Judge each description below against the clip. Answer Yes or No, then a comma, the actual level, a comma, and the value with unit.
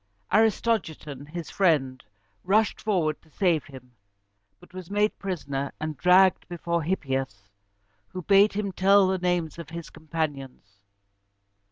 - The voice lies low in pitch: No, medium, 170 Hz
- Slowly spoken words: Yes, slow, 130 wpm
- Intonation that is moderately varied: Yes, average, 4.7 semitones